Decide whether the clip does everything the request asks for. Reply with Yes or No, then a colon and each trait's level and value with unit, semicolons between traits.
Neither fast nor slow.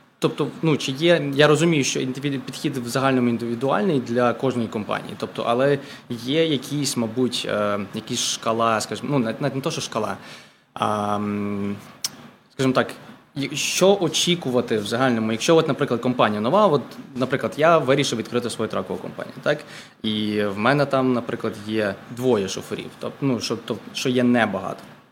Yes: average, 150 wpm